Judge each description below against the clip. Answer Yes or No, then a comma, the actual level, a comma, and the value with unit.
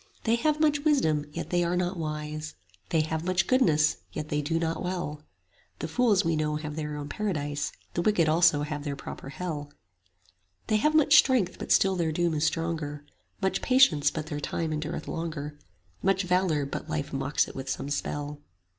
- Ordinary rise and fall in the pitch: Yes, average, 3.6 semitones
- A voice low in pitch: No, medium, 160 Hz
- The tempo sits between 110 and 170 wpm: No, average, 190 wpm